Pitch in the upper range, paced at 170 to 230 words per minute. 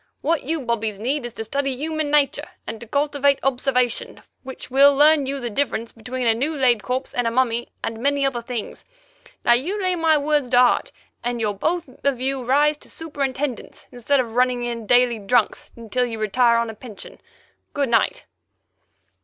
Yes: very high, 255 Hz; average, 185 wpm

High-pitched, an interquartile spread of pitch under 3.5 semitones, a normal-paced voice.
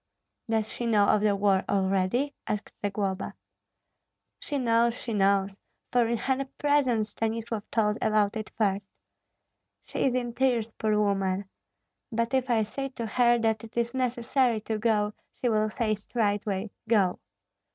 Yes: high, 220 Hz; narrow, 2.6 semitones; average, 150 wpm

